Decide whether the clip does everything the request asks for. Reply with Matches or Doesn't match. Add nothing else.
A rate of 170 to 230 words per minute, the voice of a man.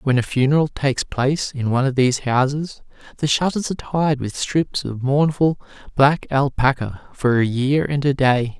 Matches